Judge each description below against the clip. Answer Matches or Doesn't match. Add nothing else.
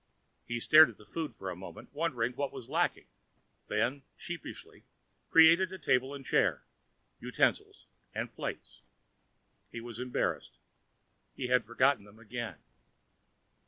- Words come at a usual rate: Doesn't match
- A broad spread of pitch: Doesn't match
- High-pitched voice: Doesn't match